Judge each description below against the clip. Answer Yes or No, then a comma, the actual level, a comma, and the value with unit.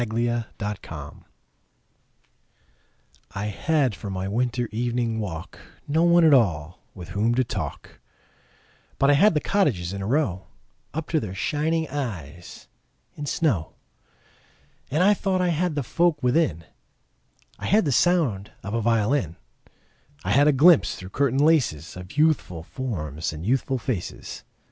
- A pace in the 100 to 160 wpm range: Yes, average, 145 wpm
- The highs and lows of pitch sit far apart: Yes, wide, 7.7 semitones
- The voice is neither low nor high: No, low, 120 Hz